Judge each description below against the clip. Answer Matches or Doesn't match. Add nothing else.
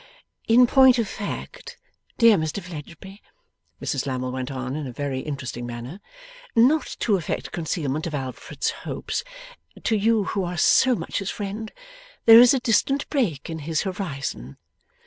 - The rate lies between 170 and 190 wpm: Doesn't match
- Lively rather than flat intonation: Matches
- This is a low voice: Doesn't match